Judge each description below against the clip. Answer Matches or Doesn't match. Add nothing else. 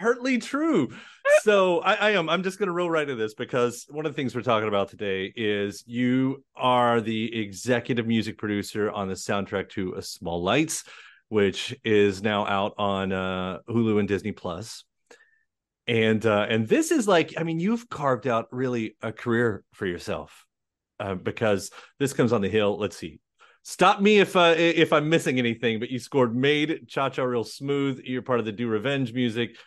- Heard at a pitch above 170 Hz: Doesn't match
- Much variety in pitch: Matches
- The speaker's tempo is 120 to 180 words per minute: Doesn't match